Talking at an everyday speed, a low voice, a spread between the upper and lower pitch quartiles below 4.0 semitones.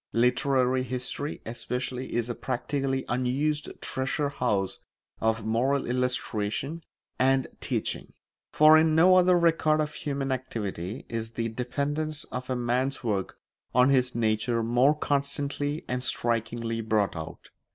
No: slow, 130 wpm; low, 125 Hz; average, 3.4 semitones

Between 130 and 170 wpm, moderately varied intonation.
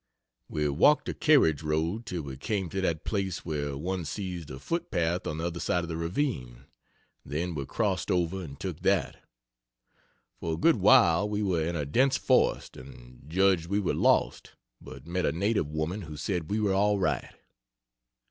No: average, 185 wpm; average, 4.3 semitones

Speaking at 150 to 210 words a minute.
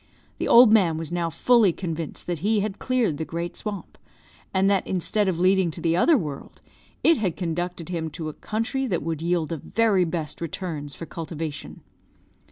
Yes: average, 185 wpm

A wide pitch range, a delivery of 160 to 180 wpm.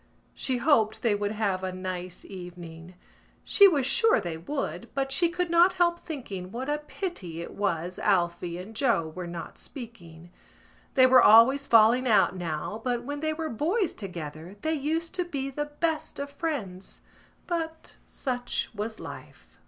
Yes: wide, 8.4 semitones; average, 165 wpm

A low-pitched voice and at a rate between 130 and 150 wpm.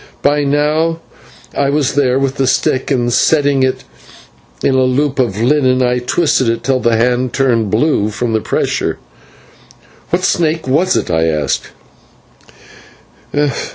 Yes: low, 130 Hz; average, 145 wpm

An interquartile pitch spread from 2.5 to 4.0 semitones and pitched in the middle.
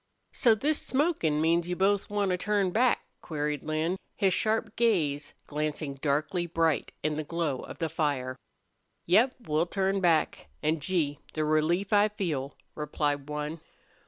No: average, 4.6 semitones; medium, 165 Hz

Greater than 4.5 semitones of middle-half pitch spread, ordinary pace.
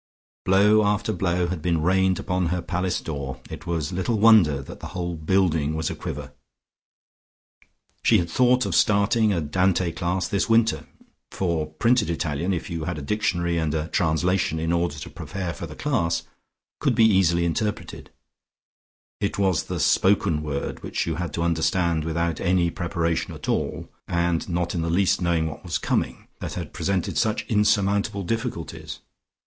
No: average, 3.1 semitones; average, 170 wpm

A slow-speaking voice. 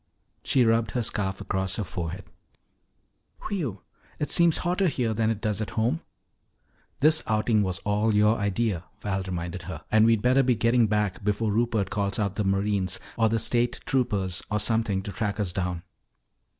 No: average, 175 wpm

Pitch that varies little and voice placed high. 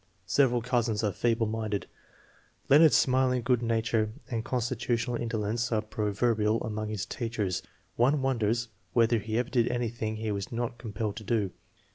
No: narrow, 2.0 semitones; low, 115 Hz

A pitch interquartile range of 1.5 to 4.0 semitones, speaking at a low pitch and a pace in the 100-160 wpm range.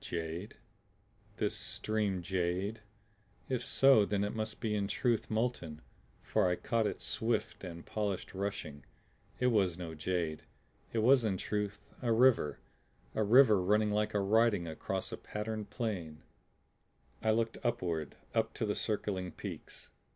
Yes: average, 3.5 semitones; low, 105 Hz; average, 145 wpm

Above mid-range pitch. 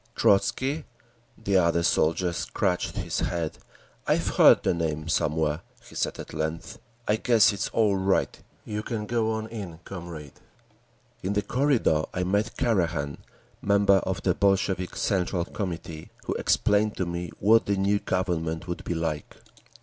No: very low, 95 Hz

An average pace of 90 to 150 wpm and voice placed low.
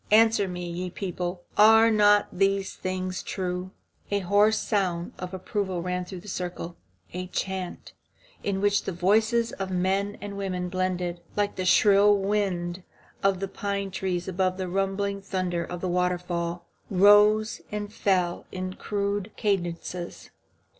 No: average, 145 wpm; high, 190 Hz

